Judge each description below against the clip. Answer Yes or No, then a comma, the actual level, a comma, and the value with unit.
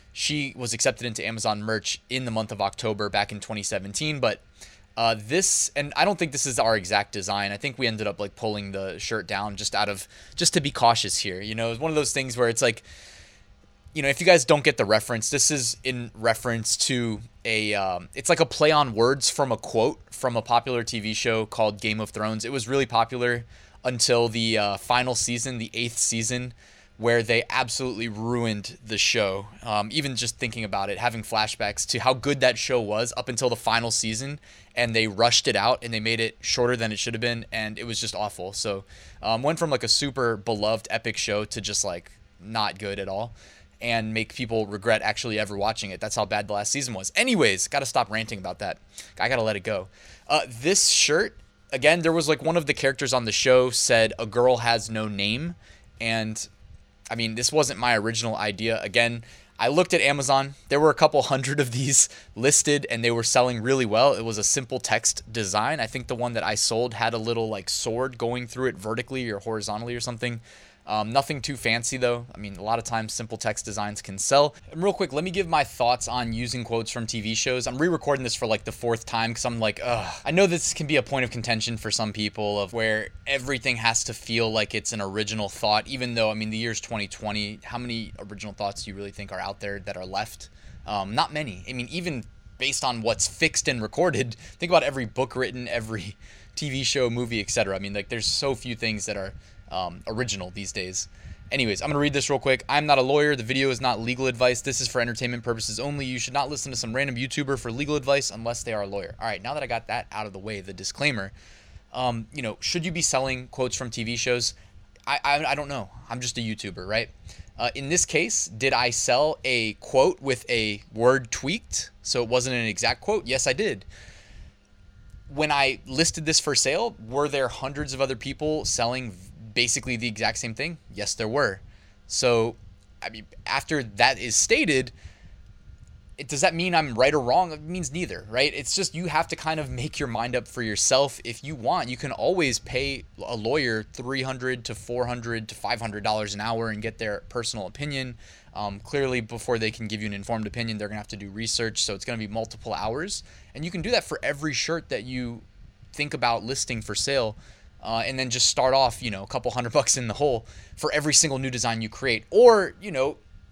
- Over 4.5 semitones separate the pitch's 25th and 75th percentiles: No, average, 3.6 semitones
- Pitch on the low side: Yes, low, 115 Hz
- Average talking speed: No, fast, 225 wpm